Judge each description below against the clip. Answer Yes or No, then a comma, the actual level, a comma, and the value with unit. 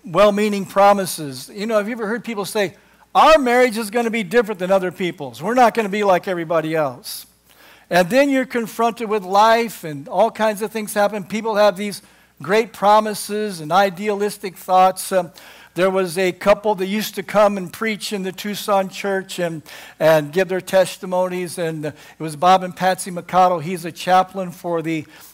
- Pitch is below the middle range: No, high, 195 Hz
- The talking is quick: No, average, 190 wpm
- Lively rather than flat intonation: No, average, 2.9 semitones